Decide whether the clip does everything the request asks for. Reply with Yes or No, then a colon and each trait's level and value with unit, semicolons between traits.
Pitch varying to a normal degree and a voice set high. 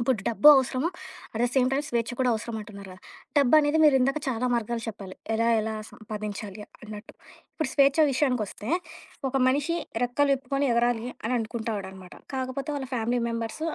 Yes: average, 3.7 semitones; high, 240 Hz